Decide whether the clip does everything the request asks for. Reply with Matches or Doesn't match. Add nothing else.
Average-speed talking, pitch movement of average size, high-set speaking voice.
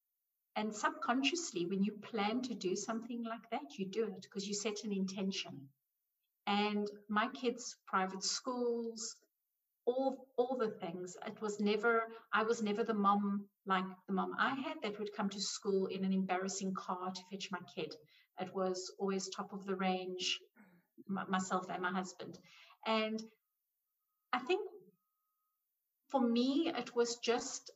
Matches